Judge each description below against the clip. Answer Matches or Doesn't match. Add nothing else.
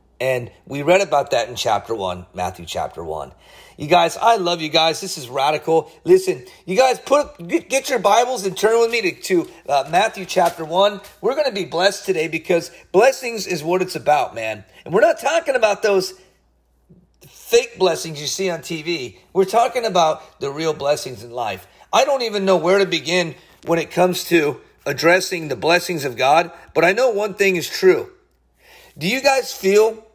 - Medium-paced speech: Matches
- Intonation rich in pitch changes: Matches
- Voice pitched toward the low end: Doesn't match